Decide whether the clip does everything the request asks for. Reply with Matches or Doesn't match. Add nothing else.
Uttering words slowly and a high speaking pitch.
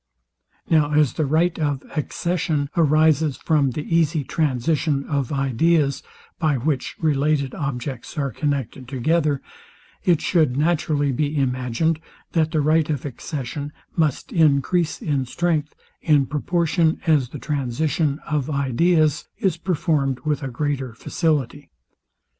Doesn't match